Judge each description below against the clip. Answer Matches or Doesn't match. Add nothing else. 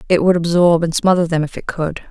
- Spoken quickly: Matches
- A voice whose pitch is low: Doesn't match